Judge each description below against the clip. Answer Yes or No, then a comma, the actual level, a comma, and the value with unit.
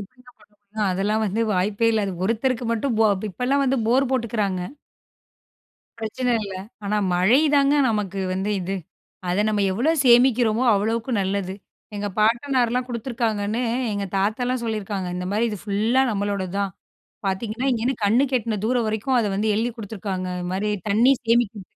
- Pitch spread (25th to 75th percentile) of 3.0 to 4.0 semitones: Yes, average, 3.3 semitones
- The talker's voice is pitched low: No, high, 220 Hz